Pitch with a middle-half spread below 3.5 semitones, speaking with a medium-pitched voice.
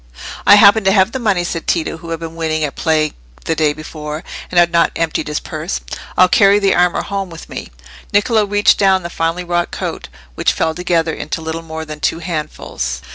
Yes: average, 3.0 semitones; medium, 165 Hz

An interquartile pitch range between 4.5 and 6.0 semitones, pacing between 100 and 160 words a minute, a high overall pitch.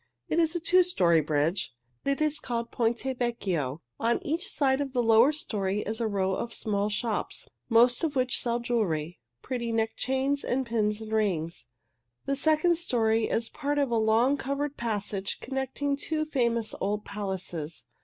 No: average, 4.9 semitones; average, 170 wpm; high, 235 Hz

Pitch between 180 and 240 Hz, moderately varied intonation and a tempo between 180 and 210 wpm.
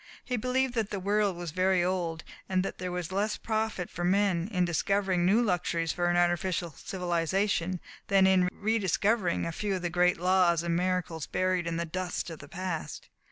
No: medium, 185 Hz; narrow, 2.2 semitones; average, 195 wpm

